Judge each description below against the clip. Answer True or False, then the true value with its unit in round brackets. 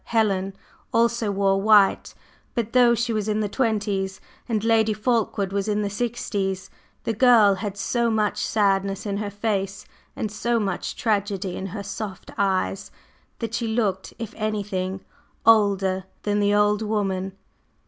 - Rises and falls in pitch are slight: True (2.2 semitones)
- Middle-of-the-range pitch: False (205 Hz)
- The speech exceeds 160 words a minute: False (150 wpm)